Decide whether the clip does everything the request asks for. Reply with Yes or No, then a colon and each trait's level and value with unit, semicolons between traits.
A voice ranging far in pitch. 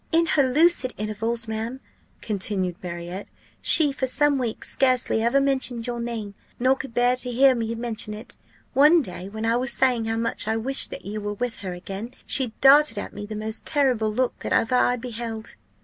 No: average, 3.2 semitones